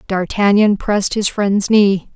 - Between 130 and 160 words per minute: Yes, average, 140 wpm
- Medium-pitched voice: No, high, 200 Hz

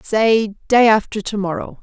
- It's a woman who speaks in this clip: Yes, female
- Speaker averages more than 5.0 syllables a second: No, 4.5 syllables/s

